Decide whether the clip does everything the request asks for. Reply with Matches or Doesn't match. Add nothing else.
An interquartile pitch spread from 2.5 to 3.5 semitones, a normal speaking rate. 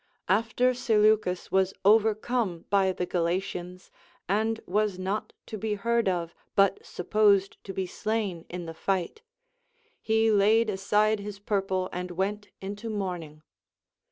Doesn't match